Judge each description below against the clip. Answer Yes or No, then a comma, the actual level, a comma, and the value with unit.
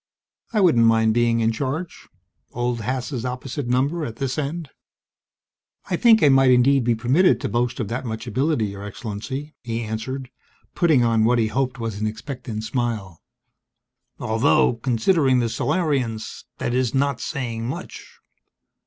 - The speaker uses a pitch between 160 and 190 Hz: No, low, 125 Hz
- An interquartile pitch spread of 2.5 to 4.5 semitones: Yes, average, 3.3 semitones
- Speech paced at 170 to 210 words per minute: No, average, 155 wpm